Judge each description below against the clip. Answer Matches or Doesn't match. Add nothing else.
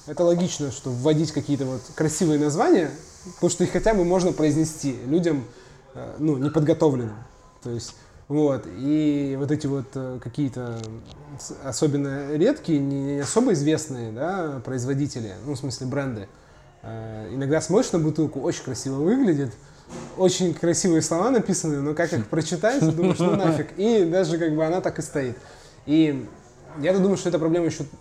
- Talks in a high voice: Doesn't match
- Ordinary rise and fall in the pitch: Matches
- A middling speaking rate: Matches